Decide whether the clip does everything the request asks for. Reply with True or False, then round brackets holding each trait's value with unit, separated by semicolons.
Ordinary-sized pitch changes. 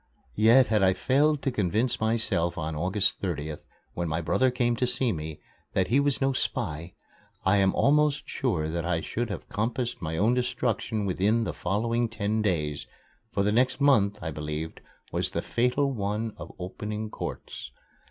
False (5.7 semitones)